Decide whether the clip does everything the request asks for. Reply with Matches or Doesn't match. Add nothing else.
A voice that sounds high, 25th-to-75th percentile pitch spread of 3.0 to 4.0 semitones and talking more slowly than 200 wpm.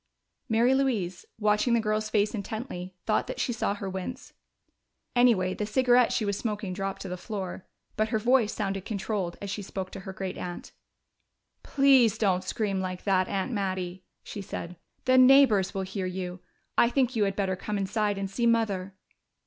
Matches